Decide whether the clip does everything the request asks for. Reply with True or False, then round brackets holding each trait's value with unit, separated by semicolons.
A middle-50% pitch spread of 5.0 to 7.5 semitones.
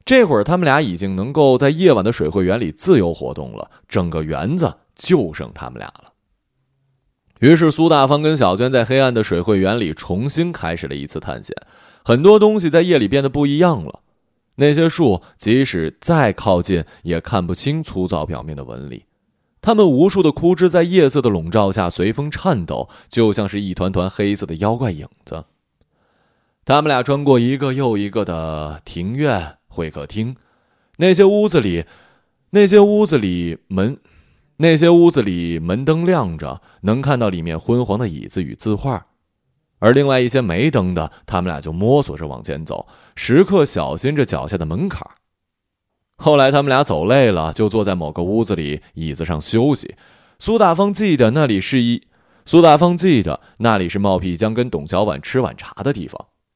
False (8.7 semitones)